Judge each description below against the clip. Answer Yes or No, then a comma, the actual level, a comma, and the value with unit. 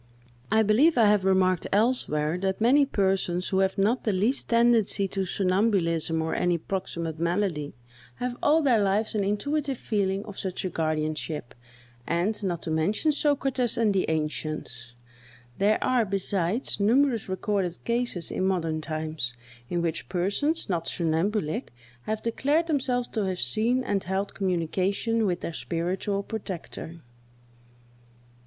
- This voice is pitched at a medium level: No, high, 195 Hz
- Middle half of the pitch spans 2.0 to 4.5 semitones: No, average, 4.9 semitones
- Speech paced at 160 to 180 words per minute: No, average, 140 wpm